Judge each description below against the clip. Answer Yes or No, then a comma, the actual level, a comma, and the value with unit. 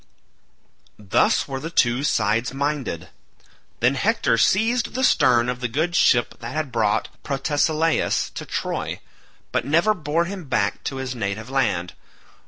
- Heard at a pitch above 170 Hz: No, low, 135 Hz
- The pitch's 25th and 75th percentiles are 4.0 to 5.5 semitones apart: Yes, average, 5.2 semitones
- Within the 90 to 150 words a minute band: Yes, average, 145 wpm